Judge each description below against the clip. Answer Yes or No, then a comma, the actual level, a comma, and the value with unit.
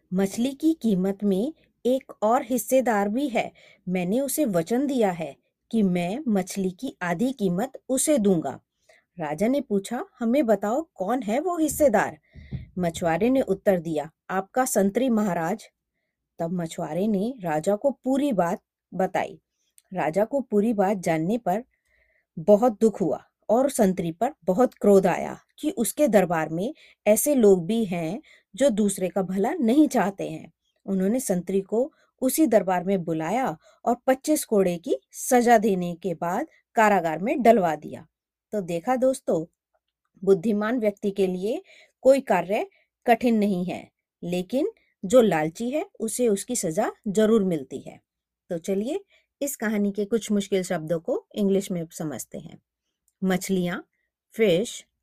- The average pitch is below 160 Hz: No, high, 210 Hz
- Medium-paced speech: Yes, average, 145 wpm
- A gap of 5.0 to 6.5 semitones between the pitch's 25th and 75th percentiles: Yes, average, 5.3 semitones